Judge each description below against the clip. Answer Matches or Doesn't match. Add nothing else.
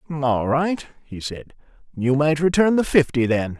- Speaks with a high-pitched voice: Doesn't match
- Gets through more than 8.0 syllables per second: Doesn't match